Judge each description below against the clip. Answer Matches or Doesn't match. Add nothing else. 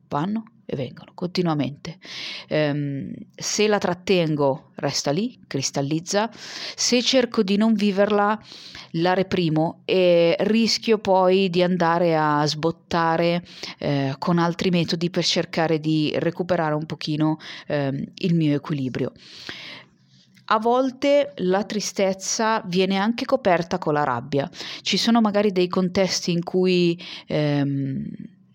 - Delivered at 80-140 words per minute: Matches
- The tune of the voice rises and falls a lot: Doesn't match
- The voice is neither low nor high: Matches